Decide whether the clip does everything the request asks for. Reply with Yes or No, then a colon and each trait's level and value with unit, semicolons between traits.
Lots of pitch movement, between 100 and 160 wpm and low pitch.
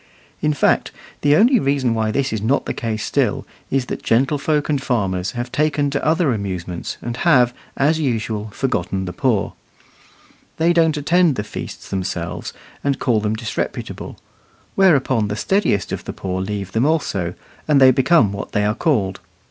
No: wide, 6.1 semitones; average, 170 wpm; low, 125 Hz